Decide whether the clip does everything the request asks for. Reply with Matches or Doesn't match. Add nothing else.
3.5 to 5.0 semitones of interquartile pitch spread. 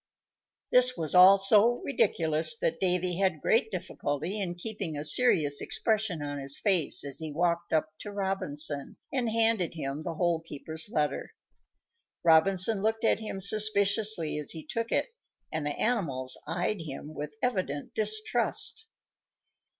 Doesn't match